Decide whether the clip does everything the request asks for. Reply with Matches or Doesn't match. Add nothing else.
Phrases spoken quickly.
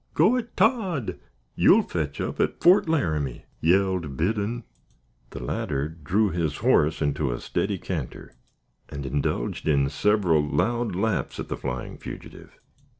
Doesn't match